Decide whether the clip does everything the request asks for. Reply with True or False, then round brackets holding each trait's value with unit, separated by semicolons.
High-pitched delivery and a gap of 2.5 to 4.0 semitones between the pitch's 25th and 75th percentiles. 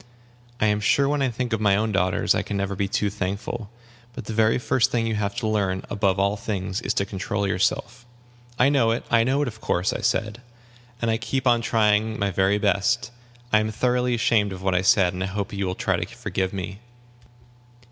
False (105 Hz; 3.0 semitones)